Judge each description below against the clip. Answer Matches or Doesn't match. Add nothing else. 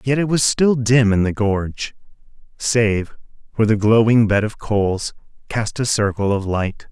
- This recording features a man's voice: Matches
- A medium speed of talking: Matches